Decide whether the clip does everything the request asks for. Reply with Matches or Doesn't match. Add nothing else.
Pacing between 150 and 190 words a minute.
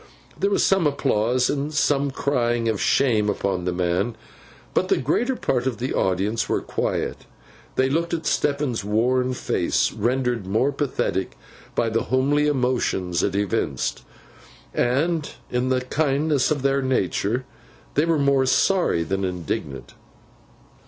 Doesn't match